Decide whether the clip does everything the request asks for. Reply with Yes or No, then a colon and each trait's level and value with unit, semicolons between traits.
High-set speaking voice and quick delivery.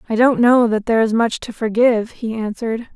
Yes: high, 230 Hz; fast, 225 wpm